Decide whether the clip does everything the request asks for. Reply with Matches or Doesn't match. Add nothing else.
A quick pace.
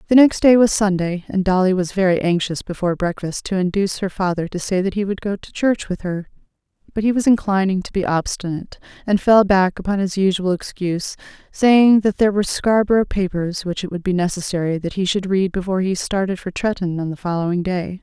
Matches